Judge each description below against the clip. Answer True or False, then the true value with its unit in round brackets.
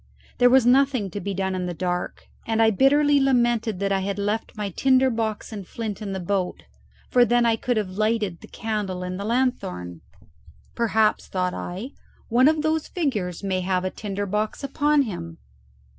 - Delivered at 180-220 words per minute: True (190 wpm)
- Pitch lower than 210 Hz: False (215 Hz)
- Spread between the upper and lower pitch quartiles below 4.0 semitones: False (4.5 semitones)